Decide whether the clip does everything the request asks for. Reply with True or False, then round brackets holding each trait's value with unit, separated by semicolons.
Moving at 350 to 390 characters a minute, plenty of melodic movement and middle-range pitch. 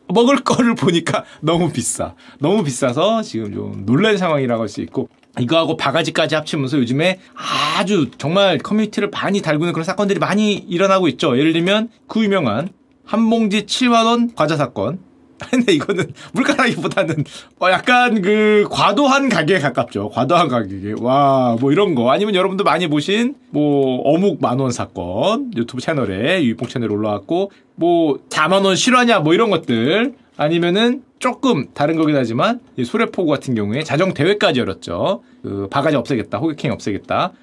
True (355 characters per minute; 8.1 semitones; 175 Hz)